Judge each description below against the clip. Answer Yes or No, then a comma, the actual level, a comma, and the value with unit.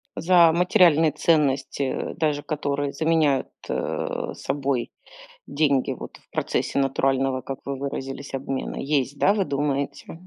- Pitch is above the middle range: No, medium, 140 Hz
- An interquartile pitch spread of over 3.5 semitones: No, narrow, 2.6 semitones